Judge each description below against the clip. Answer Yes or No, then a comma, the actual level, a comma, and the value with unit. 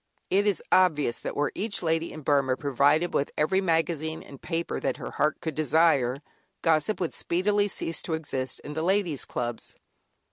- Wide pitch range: No, average, 3.4 semitones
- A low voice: No, medium, 160 Hz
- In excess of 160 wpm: Yes, average, 175 wpm